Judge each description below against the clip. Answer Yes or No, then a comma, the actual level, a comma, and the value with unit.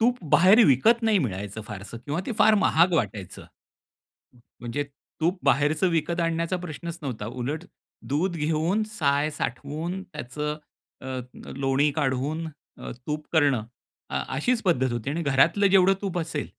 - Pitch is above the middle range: No, medium, 150 Hz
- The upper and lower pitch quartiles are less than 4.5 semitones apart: No, average, 4.9 semitones